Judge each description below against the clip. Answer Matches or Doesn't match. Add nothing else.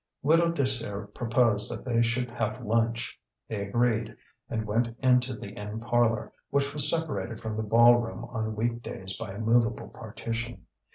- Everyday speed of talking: Matches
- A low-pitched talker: Matches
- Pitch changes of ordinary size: Doesn't match